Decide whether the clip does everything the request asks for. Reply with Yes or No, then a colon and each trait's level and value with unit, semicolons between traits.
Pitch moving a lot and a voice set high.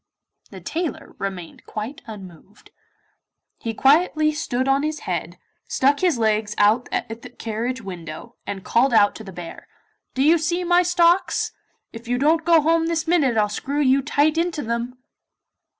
Yes: wide, 6.5 semitones; very high, 260 Hz